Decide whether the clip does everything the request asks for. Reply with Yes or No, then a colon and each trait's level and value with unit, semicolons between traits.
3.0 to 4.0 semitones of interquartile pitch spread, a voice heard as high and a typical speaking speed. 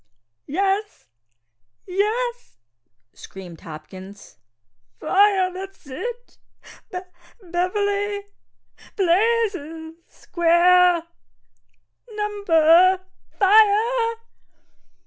No: average, 3.6 semitones; very high, 375 Hz; slow, 60 wpm